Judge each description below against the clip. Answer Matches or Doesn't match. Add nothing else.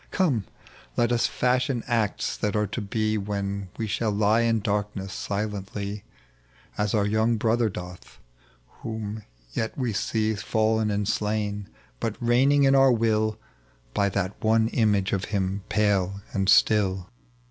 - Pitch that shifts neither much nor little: Doesn't match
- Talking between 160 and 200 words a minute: Doesn't match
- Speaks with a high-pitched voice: Doesn't match